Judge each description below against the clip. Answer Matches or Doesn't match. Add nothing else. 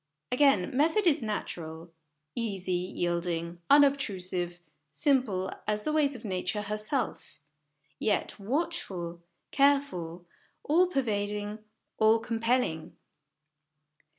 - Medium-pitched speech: Doesn't match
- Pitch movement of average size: Doesn't match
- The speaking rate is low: Matches